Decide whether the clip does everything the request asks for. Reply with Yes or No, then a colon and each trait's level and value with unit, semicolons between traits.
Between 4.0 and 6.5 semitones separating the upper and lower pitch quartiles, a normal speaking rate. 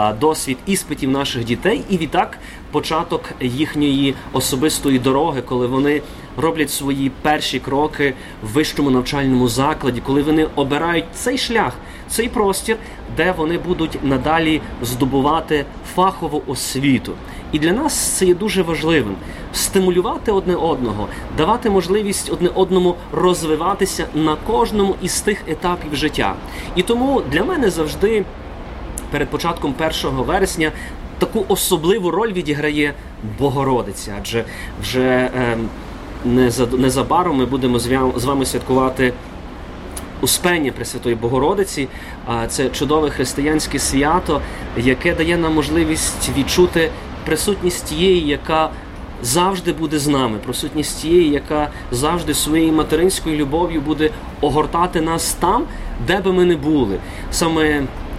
Yes: average, 4.8 semitones; average, 120 wpm